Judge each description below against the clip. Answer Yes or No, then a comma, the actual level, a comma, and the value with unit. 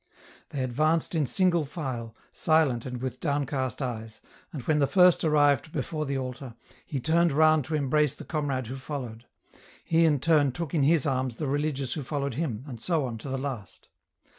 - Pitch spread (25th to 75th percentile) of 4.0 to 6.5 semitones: No, average, 3.3 semitones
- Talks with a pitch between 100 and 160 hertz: Yes, medium, 140 Hz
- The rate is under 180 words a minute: No, average, 190 wpm